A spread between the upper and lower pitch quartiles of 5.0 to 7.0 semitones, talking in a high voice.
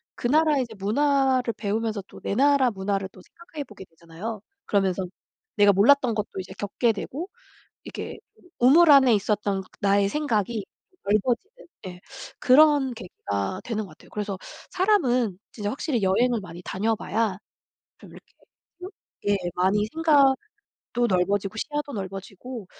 Yes: wide, 5.4 semitones; high, 220 Hz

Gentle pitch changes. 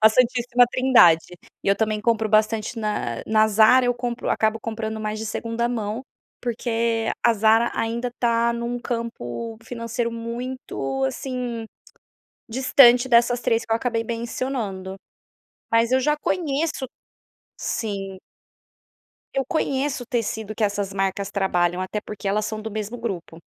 Yes: narrow, 2.3 semitones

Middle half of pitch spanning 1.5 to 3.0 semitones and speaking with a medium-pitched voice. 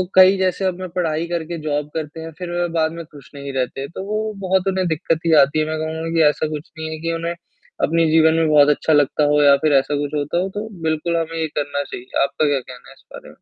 Yes: narrow, 2.5 semitones; medium, 160 Hz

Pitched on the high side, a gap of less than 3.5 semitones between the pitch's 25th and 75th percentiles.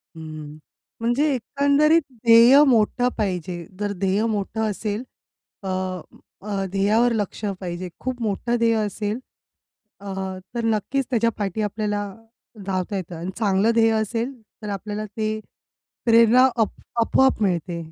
Yes: high, 215 Hz; average, 3.1 semitones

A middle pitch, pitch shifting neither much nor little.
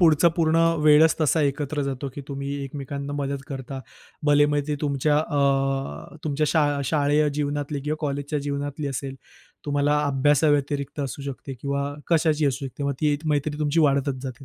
No: medium, 145 Hz; narrow, 1.3 semitones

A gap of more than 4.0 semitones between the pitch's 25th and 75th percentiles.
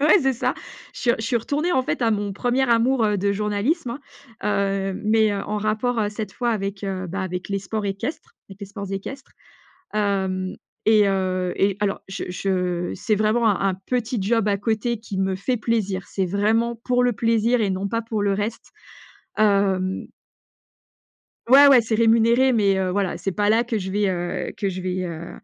No: average, 3.1 semitones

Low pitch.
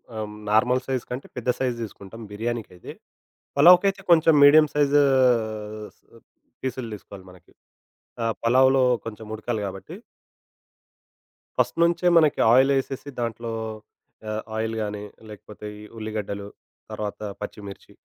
Yes: low, 115 Hz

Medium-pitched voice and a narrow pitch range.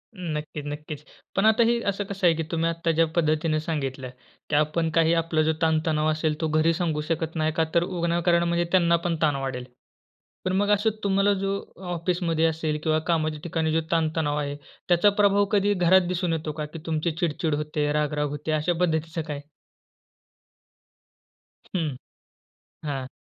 Yes: medium, 160 Hz; narrow, 2.1 semitones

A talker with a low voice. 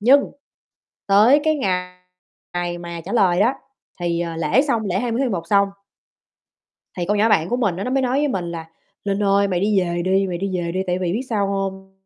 No: high, 195 Hz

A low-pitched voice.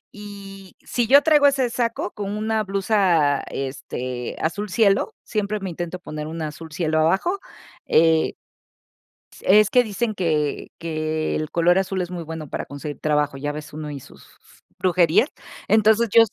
No: medium, 180 Hz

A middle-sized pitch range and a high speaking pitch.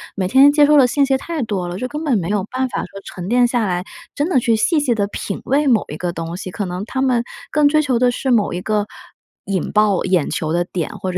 No: wide, 6.4 semitones; high, 225 Hz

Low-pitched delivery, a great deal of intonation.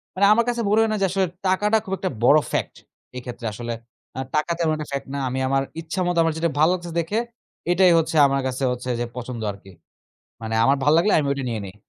No: medium, 155 Hz; wide, 6.5 semitones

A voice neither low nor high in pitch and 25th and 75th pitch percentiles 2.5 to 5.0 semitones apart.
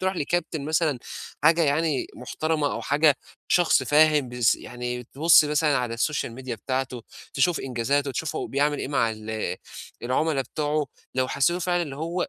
Yes: medium, 145 Hz; average, 3.7 semitones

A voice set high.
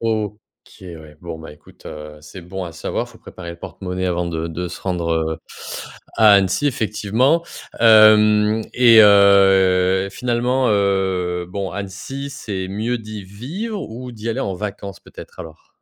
No: low, 100 Hz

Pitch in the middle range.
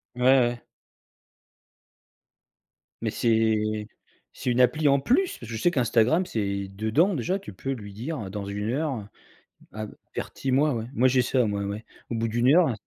No: low, 120 Hz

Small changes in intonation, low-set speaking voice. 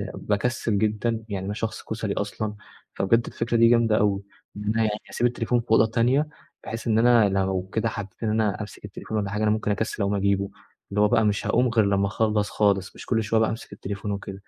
Yes: narrow, 2.0 semitones; low, 110 Hz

